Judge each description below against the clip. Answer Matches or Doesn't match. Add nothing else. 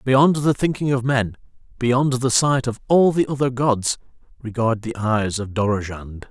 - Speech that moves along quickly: Doesn't match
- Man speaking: Matches